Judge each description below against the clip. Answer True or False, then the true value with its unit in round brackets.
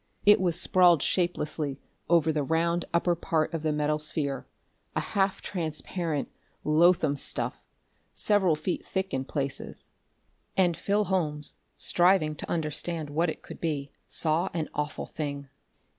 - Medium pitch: True (160 Hz)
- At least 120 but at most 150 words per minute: True (140 wpm)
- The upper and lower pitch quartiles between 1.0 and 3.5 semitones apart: True (2.9 semitones)